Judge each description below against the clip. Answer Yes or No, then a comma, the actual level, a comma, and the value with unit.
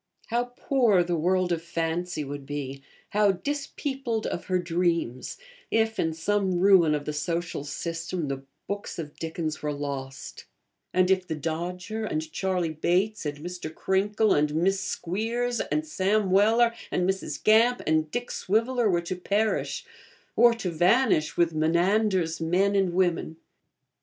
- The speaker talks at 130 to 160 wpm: Yes, average, 150 wpm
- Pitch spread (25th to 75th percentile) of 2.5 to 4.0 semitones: No, average, 4.6 semitones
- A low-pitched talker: No, medium, 180 Hz